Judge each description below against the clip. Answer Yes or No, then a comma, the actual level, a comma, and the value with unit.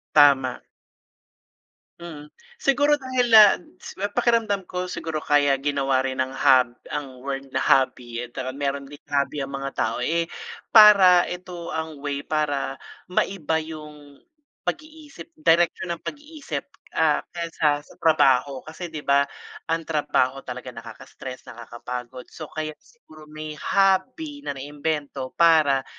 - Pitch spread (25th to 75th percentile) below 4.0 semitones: No, average, 4.4 semitones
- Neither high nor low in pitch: Yes, medium, 150 Hz